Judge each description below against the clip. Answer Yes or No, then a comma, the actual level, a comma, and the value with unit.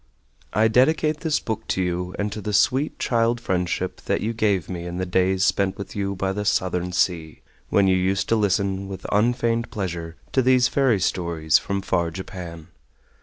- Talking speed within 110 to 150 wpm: No, average, 185 wpm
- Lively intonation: No, average, 3.7 semitones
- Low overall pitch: Yes, very low, 95 Hz